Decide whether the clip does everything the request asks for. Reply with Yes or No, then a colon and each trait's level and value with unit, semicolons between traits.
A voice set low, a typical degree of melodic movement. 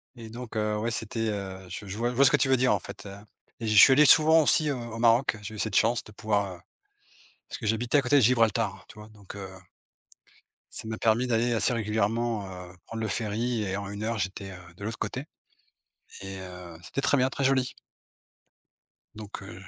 Yes: low, 110 Hz; average, 3.2 semitones